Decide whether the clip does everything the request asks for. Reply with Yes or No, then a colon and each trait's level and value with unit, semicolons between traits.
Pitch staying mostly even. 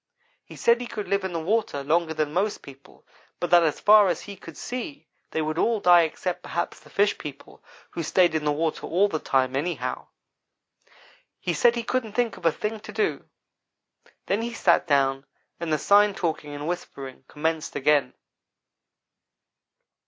No: wide, 5.4 semitones